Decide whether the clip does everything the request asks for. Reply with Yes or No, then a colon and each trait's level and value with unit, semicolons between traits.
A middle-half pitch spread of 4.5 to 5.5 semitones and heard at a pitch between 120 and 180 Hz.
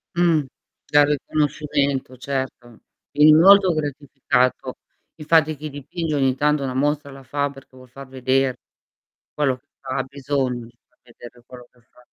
No: narrow, 2.5 semitones; medium, 140 Hz